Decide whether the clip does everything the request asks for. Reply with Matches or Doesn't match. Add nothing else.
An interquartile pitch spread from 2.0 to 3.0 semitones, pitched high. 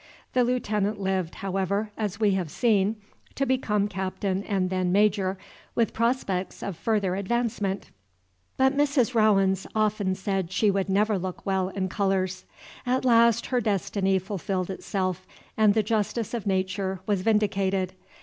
Matches